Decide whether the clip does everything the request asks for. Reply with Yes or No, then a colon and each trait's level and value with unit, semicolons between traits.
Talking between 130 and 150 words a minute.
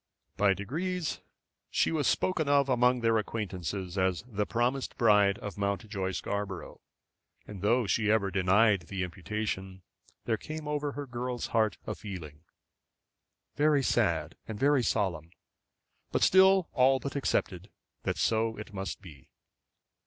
Yes: average, 140 wpm